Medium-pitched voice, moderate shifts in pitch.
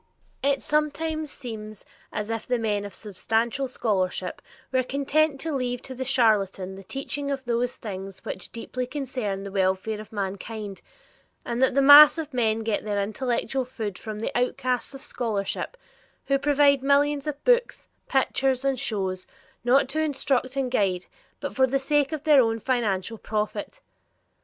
No: very high, 250 Hz; average, 4.6 semitones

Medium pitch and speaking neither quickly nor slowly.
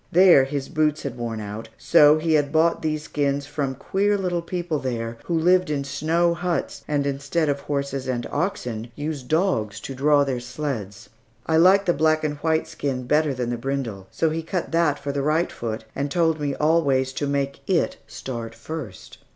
Yes: medium, 145 Hz; average, 190 wpm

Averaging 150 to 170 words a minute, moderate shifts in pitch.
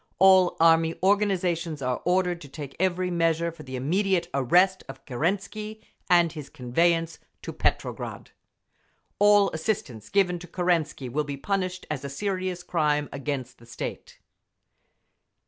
No: slow, 135 wpm; average, 4.2 semitones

